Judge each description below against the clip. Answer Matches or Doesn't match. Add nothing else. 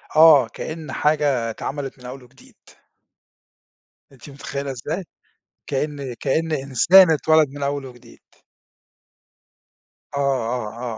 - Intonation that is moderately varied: Matches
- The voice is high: Doesn't match